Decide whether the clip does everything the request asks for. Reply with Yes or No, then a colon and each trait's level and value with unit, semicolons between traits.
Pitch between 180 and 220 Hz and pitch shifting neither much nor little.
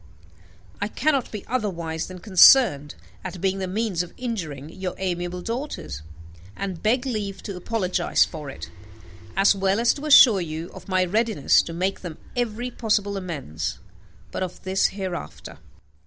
Yes: high, 190 Hz; average, 4.1 semitones